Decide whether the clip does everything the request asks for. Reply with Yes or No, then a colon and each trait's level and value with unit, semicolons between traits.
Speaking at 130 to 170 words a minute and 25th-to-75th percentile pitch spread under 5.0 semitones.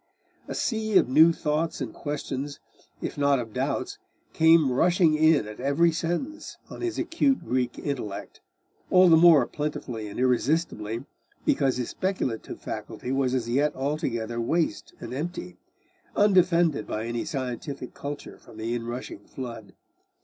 No: average, 140 wpm; wide, 5.4 semitones